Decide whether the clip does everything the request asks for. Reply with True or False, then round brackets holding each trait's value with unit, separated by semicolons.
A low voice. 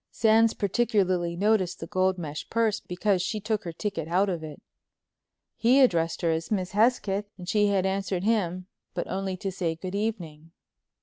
False (190 Hz)